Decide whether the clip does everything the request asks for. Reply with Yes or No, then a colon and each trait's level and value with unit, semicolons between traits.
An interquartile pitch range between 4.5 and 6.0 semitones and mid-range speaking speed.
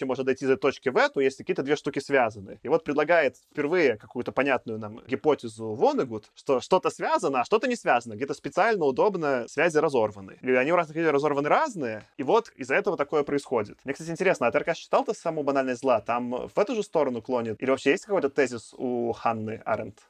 No: average, 5.2 semitones; fast, 205 wpm